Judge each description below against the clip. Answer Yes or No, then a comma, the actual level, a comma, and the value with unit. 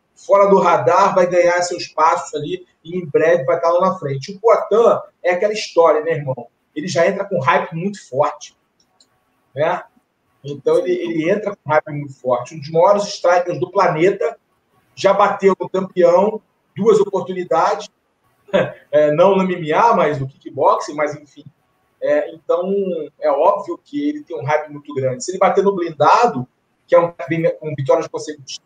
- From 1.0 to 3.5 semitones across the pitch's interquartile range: No, average, 4.1 semitones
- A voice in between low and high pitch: Yes, medium, 175 Hz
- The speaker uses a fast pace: No, average, 170 wpm